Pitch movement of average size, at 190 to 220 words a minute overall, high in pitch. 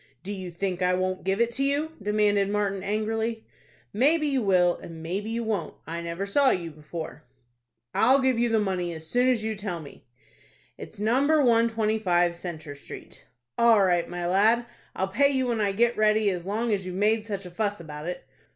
Yes: average, 4.3 semitones; average, 195 wpm; high, 205 Hz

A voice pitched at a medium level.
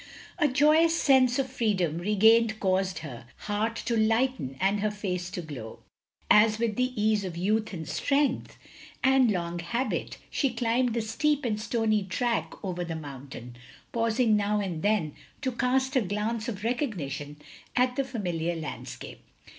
No: high, 215 Hz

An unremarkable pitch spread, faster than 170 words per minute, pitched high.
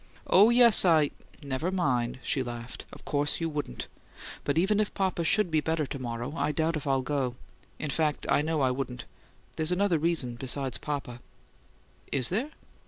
No: average, 4.4 semitones; average, 180 wpm; medium, 150 Hz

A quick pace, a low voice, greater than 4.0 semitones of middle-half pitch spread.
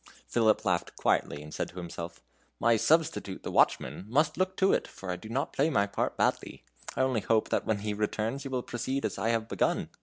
Yes: fast, 215 wpm; low, 115 Hz; average, 5.1 semitones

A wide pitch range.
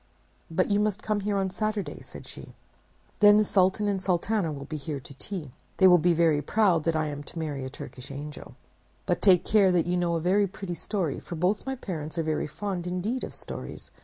No: average, 4.5 semitones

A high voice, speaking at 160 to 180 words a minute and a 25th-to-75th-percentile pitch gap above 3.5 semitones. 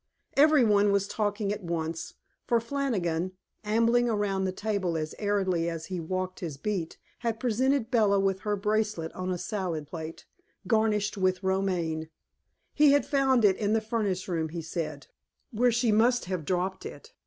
Yes: high, 200 Hz; average, 165 wpm; average, 4.1 semitones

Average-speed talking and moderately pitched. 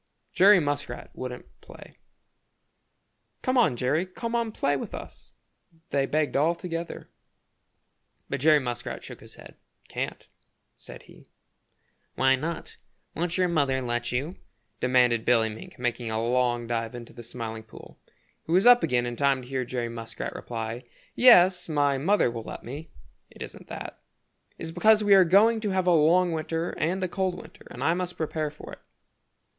Yes: average, 165 wpm; medium, 145 Hz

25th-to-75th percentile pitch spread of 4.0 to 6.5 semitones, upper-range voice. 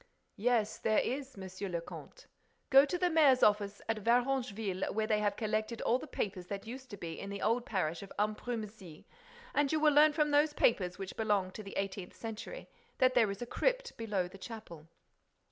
Yes: average, 4.7 semitones; high, 215 Hz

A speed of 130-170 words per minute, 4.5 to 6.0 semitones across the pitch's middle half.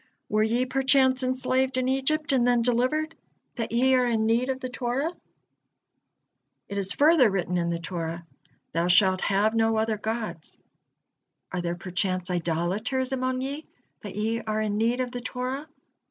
Yes: average, 165 wpm; average, 4.8 semitones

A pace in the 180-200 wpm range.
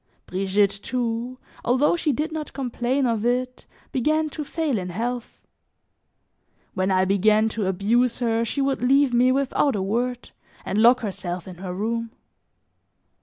No: average, 150 wpm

